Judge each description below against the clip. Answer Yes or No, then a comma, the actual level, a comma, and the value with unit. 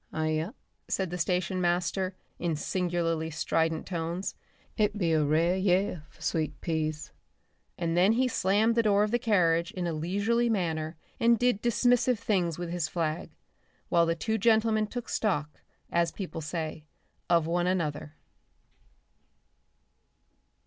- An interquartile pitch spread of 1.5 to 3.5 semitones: No, average, 4.3 semitones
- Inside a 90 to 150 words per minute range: Yes, average, 145 wpm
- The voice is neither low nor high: Yes, medium, 175 Hz